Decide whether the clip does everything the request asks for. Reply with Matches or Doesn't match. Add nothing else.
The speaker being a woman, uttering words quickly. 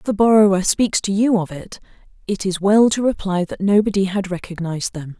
Matches